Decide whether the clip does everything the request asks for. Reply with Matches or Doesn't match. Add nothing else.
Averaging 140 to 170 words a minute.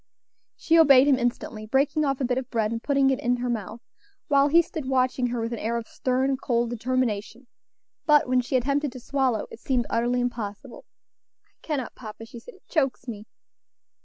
Doesn't match